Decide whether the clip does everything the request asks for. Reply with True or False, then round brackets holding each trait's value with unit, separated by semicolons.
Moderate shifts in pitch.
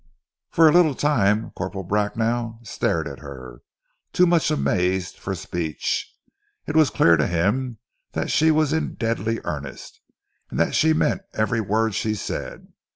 False (8.3 semitones)